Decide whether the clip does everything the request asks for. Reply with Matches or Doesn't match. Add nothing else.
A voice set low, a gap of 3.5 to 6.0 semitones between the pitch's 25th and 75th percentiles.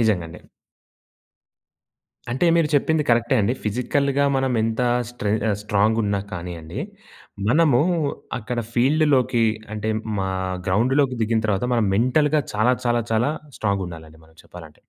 Matches